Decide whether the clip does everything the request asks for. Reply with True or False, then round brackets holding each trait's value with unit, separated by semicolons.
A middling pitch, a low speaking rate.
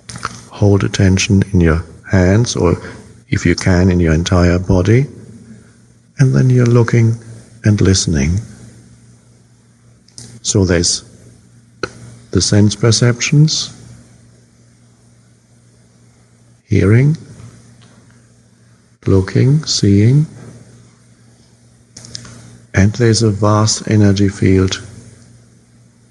False (100 Hz; 75 wpm)